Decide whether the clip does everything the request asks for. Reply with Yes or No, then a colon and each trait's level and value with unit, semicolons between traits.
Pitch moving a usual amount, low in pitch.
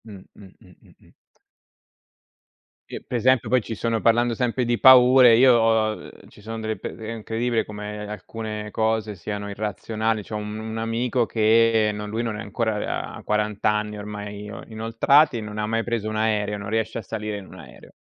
No: narrow, 1.4 semitones; low, 110 Hz